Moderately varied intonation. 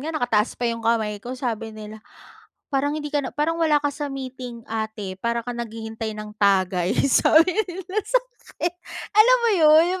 No: wide, 5.9 semitones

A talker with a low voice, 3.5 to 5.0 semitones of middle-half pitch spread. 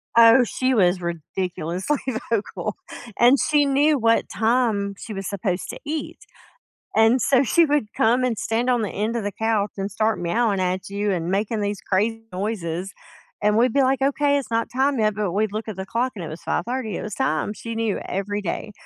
No: high, 220 Hz; average, 3.9 semitones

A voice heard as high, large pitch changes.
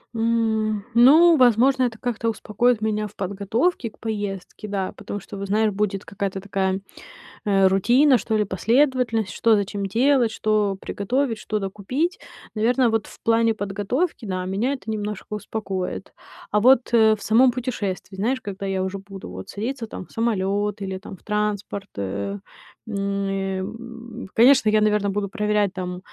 No: high, 210 Hz; average, 3.0 semitones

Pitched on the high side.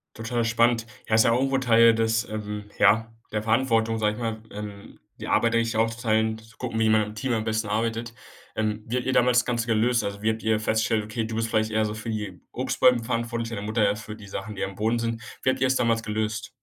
No: low, 110 Hz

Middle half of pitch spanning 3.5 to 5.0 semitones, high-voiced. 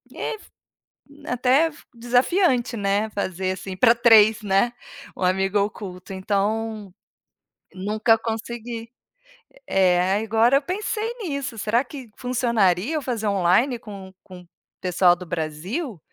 Yes: average, 4.3 semitones; high, 220 Hz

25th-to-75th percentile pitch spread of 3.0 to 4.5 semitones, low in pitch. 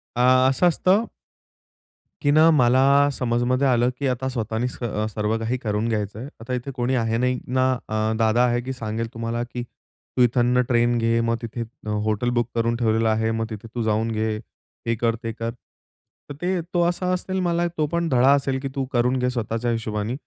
No: narrow, 2.6 semitones; low, 120 Hz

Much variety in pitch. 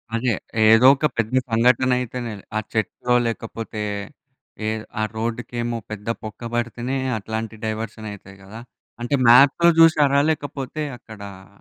No: narrow, 2.6 semitones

